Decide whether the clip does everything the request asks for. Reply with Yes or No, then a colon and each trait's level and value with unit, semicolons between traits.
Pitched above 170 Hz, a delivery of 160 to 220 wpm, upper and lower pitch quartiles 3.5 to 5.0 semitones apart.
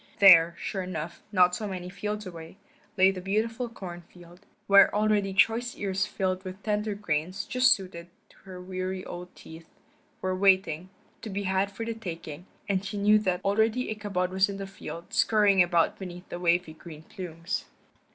No: high, 190 Hz; average, 170 wpm; narrow, 2.5 semitones